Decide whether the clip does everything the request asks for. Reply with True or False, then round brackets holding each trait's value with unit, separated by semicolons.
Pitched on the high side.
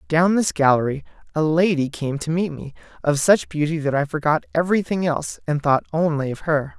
False (155 Hz)